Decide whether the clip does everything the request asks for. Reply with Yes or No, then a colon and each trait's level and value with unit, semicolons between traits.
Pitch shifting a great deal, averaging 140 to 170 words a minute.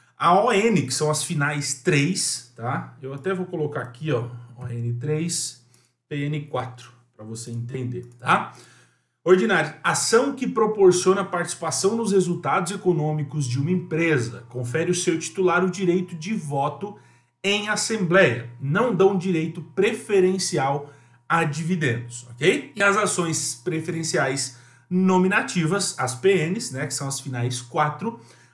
No: wide, 6.4 semitones; average, 130 wpm